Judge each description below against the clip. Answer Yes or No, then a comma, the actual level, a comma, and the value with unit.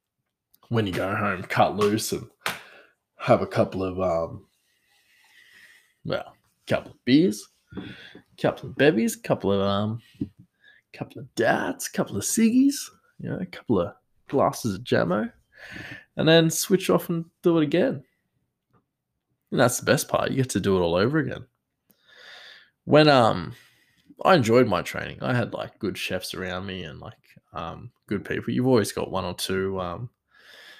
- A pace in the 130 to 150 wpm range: No, average, 165 wpm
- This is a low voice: Yes, low, 115 Hz